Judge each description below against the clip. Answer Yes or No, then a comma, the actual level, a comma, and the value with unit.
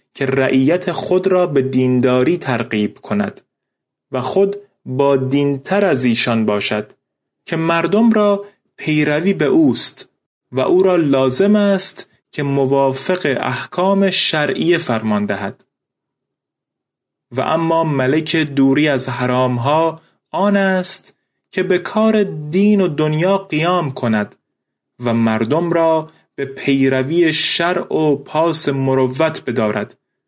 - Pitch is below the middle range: No, medium, 155 Hz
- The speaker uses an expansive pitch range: Yes, wide, 5.7 semitones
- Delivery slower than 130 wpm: Yes, average, 115 wpm